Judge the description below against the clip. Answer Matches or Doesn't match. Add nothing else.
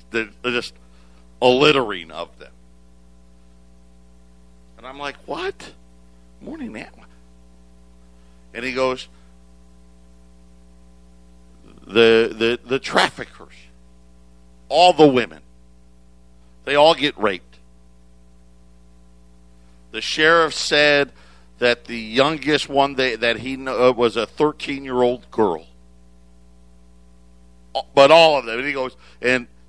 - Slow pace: Matches